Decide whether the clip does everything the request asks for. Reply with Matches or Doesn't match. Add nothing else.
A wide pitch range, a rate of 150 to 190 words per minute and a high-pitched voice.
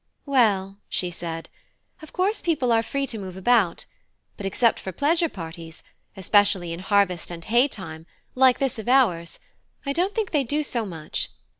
Matches